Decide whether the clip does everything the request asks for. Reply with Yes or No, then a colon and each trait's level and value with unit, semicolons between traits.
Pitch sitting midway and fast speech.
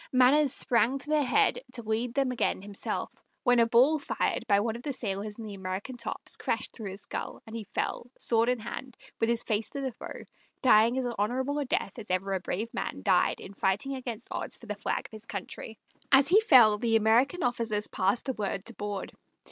No: high, 230 Hz; fast, 220 wpm